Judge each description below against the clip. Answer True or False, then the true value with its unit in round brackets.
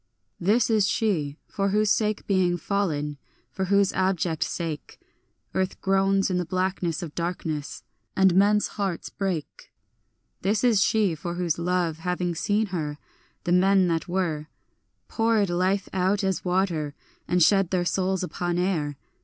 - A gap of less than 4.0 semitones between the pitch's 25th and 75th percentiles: True (2.4 semitones)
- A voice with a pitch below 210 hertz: True (185 Hz)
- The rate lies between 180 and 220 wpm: False (145 wpm)